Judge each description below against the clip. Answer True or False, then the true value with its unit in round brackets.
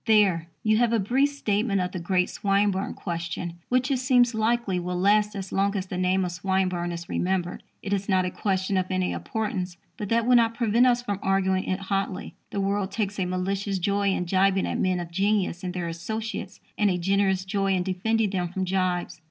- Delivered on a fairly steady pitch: True (2.3 semitones)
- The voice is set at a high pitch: True (195 Hz)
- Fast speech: True (210 wpm)